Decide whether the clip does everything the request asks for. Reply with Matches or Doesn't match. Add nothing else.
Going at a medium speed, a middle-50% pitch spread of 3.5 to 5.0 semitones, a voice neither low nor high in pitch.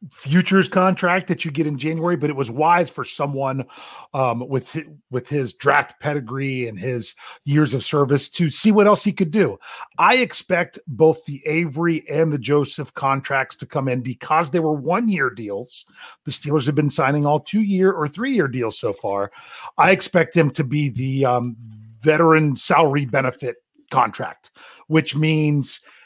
Matches